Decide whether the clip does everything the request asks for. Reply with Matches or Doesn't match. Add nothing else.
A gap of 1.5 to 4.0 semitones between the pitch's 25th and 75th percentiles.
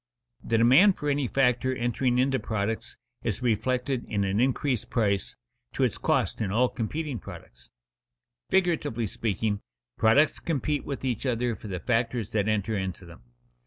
Matches